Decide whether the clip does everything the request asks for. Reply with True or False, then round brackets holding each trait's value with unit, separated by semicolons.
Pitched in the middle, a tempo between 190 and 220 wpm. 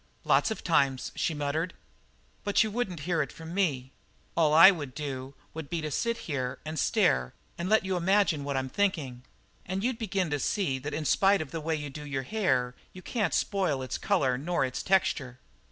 True (160 Hz; 200 wpm)